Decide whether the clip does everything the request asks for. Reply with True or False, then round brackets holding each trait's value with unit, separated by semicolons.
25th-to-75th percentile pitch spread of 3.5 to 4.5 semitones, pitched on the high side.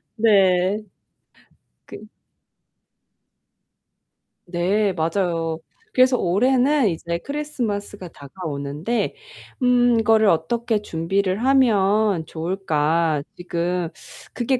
False (5.4 semitones; 195 Hz)